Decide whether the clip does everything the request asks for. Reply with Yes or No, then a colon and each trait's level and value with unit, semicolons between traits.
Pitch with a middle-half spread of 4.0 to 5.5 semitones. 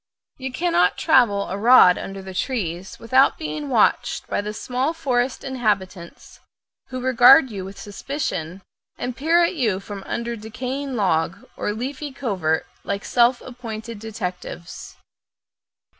Yes: average, 4.9 semitones